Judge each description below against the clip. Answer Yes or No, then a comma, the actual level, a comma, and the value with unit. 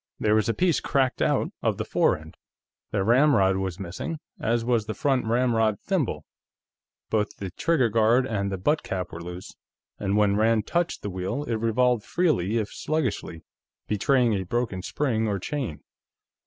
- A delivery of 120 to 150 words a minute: No, average, 170 wpm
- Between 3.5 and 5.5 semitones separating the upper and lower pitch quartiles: Yes, average, 4.6 semitones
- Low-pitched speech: Yes, low, 110 Hz